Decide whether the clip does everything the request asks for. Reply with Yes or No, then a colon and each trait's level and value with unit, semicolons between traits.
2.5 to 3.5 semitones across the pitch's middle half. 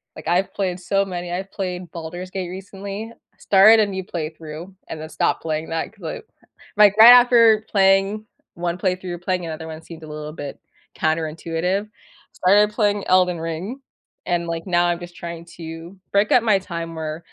Yes: average, 3.1 semitones